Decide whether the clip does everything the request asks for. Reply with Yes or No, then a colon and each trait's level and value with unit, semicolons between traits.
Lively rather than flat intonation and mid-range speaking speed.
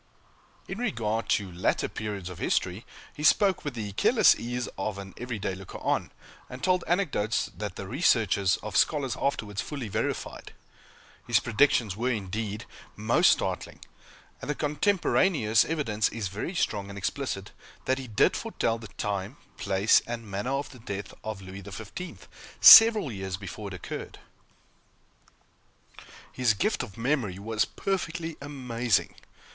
Yes: wide, 6.0 semitones; average, 145 wpm